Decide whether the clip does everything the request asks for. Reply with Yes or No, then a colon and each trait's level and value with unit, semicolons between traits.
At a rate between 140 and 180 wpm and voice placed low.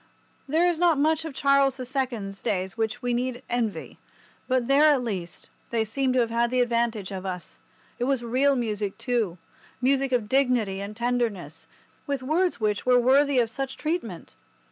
No: average, 170 wpm; high, 245 Hz